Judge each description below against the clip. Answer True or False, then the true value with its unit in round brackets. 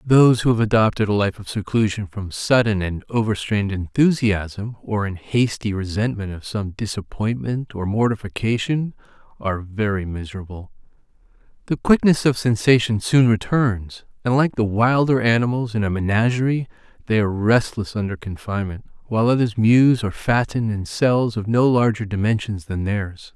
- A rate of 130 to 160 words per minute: True (145 wpm)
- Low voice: True (110 Hz)